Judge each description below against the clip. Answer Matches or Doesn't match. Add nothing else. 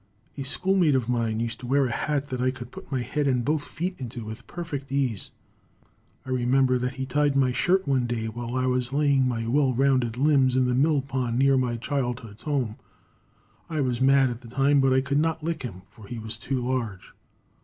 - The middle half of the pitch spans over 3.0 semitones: Doesn't match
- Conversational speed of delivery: Doesn't match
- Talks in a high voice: Doesn't match